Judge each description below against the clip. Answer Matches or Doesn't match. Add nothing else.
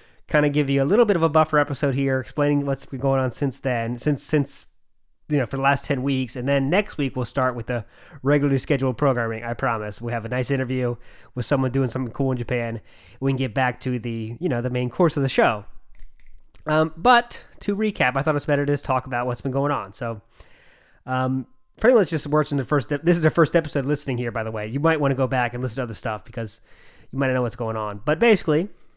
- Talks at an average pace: Doesn't match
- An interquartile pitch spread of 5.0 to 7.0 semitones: Doesn't match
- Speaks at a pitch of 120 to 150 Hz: Matches